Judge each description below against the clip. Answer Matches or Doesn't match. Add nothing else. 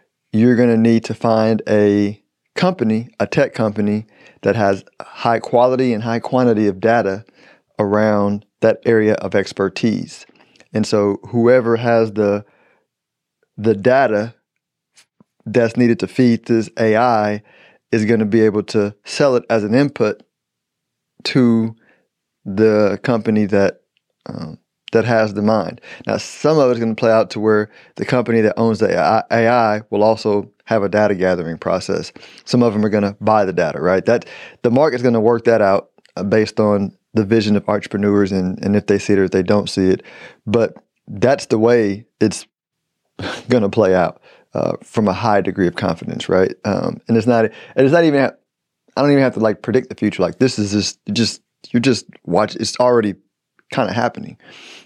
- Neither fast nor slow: Matches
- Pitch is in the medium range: Doesn't match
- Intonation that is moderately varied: Doesn't match